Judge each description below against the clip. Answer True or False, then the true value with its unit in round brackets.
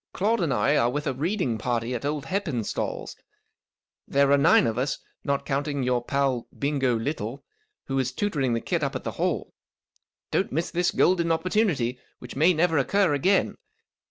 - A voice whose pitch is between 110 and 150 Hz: True (140 Hz)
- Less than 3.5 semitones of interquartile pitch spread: False (4.9 semitones)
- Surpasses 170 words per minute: True (180 wpm)